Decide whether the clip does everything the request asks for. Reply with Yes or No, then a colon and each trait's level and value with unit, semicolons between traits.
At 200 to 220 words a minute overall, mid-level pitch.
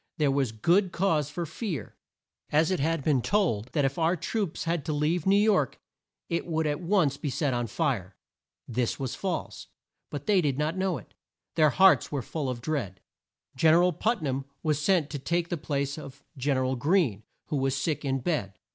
Yes: fast, 205 wpm; medium, 150 Hz